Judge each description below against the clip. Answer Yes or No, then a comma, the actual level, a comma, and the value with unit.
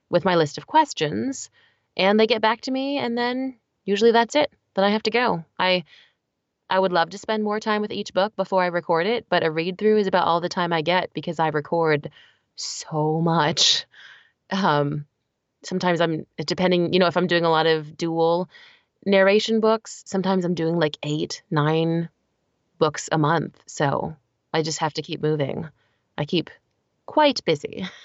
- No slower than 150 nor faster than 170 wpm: No, average, 185 wpm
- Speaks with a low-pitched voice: No, medium, 175 Hz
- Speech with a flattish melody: No, average, 4.6 semitones